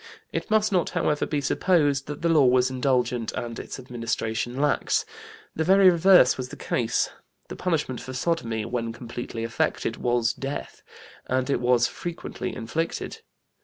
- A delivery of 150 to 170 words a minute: Yes, average, 155 wpm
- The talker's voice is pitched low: Yes, low, 130 Hz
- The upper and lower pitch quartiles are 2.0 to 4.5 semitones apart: No, average, 5.0 semitones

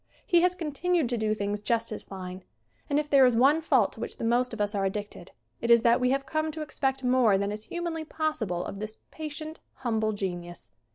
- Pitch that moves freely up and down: Yes, wide, 6.3 semitones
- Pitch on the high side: Yes, high, 240 Hz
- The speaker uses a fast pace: Yes, fast, 230 wpm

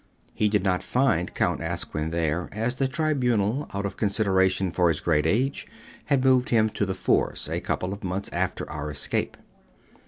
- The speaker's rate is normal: Yes, average, 180 wpm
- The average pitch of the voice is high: No, low, 100 Hz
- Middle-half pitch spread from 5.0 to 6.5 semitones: Yes, wide, 5.6 semitones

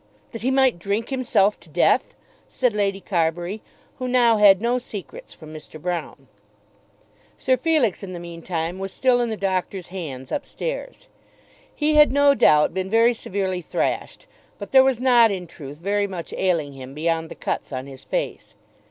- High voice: Yes, high, 195 Hz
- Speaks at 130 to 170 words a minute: No, average, 180 wpm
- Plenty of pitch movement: Yes, wide, 6.3 semitones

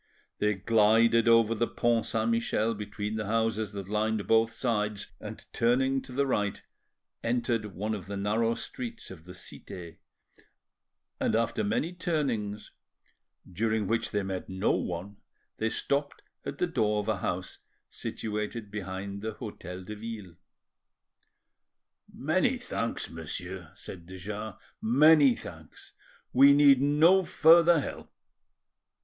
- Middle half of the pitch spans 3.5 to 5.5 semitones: No, average, 2.8 semitones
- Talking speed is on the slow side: Yes, slow, 130 wpm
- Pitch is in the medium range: No, low, 110 Hz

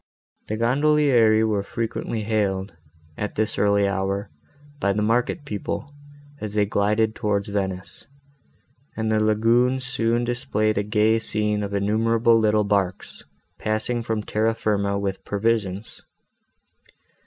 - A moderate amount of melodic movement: No, narrow, 2.0 semitones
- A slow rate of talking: Yes, slow, 130 wpm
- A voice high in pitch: No, low, 110 Hz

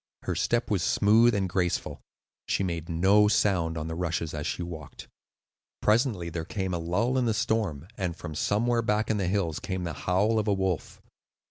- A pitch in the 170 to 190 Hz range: No, very low, 95 Hz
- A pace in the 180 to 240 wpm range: Yes, average, 195 wpm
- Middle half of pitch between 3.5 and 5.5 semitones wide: Yes, average, 4.0 semitones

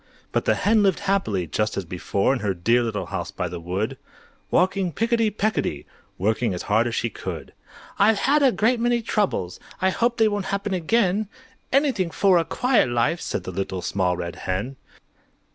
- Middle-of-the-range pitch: Yes, medium, 170 Hz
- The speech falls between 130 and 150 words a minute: No, average, 185 wpm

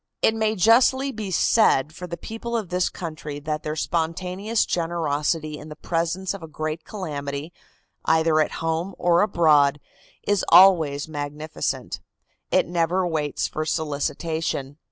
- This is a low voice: No, medium, 165 Hz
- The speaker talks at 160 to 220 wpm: No, average, 140 wpm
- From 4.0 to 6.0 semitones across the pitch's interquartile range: No, average, 3.3 semitones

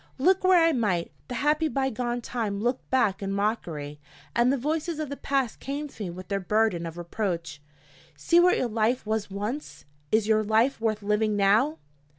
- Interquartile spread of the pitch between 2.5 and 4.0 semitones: No, average, 5.2 semitones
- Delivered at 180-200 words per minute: Yes, average, 190 wpm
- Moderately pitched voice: No, high, 220 Hz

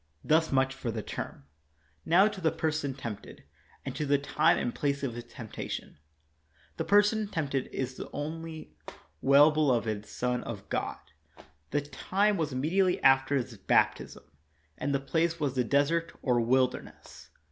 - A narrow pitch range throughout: No, average, 4.1 semitones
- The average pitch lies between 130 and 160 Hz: Yes, medium, 140 Hz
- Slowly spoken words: No, average, 160 wpm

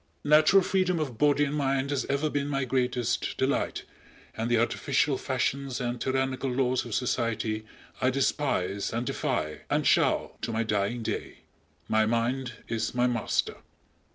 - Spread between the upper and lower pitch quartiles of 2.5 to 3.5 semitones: Yes, average, 3.1 semitones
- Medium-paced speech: Yes, average, 155 wpm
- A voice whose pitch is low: Yes, low, 130 Hz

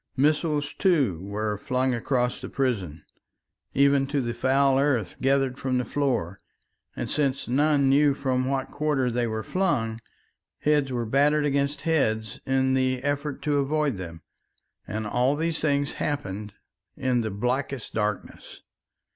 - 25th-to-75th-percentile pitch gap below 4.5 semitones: Yes, average, 3.5 semitones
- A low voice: Yes, low, 130 Hz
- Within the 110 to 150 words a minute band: Yes, average, 145 wpm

